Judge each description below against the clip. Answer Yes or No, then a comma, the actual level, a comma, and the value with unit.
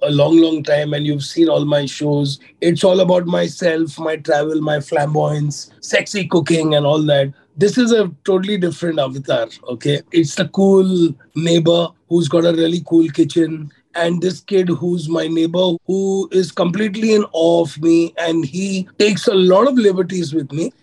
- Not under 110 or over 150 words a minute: No, average, 180 wpm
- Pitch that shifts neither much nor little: Yes, average, 3.3 semitones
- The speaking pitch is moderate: Yes, medium, 165 Hz